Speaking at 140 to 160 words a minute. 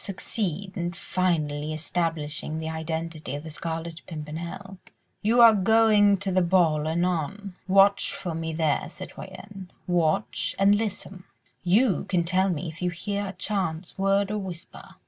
Yes: average, 145 wpm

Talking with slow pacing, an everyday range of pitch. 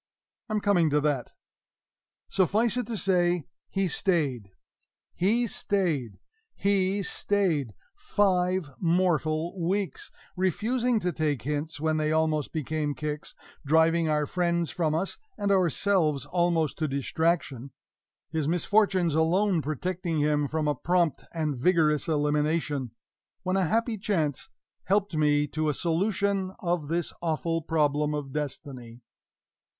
Yes: slow, 125 wpm; average, 3.9 semitones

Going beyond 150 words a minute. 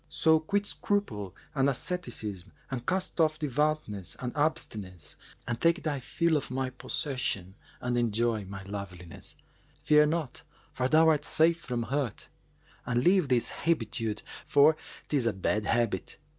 No: average, 145 wpm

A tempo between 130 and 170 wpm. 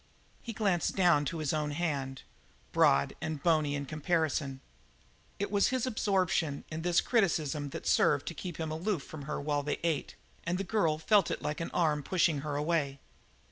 No: average, 180 wpm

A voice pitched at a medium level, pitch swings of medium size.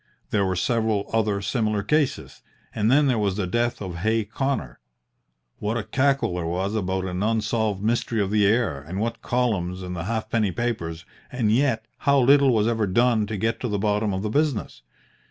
No: low, 110 Hz; average, 3.3 semitones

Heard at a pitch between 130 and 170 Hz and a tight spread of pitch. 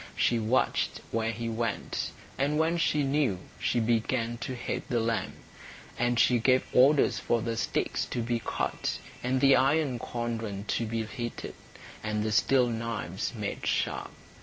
No: low, 120 Hz; narrow, 2.3 semitones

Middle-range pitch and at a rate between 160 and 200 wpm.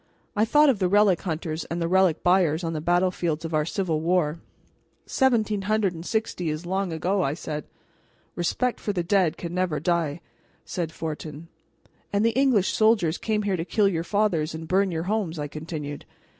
Yes: medium, 175 Hz; average, 185 wpm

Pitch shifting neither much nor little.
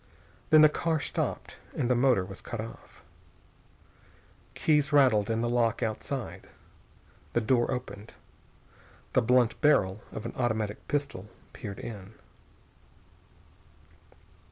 Yes: average, 3.8 semitones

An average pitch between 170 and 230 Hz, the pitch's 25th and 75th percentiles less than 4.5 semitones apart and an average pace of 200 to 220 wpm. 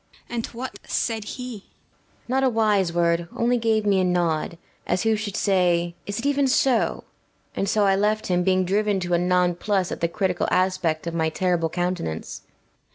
Yes: high, 190 Hz; average, 3.7 semitones; fast, 205 wpm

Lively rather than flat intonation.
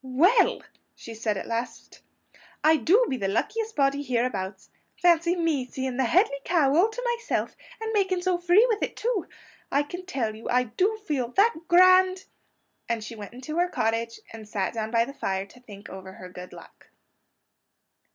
Yes: wide, 8.3 semitones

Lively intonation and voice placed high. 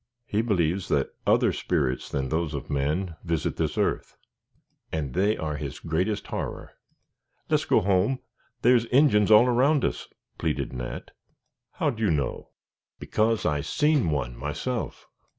No: wide, 7.4 semitones; very low, 90 Hz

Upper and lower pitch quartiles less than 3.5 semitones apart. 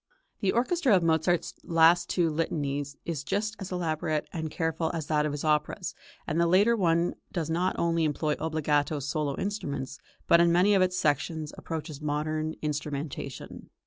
Yes: narrow, 2.6 semitones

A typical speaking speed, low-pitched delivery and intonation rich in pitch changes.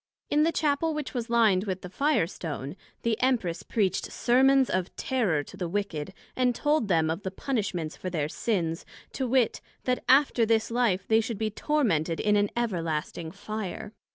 No: average, 180 wpm; high, 215 Hz; wide, 6.1 semitones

